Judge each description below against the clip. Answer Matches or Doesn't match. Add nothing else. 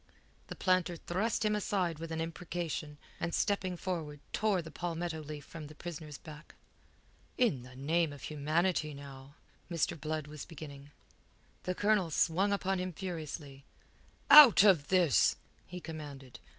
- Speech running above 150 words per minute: Doesn't match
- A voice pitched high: Doesn't match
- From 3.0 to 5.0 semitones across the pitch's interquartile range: Matches